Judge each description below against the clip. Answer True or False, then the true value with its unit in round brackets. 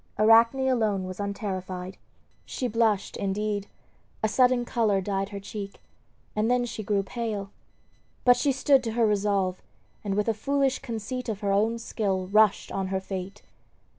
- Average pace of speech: True (160 wpm)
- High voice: True (210 Hz)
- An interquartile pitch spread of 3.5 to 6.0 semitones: False (3.0 semitones)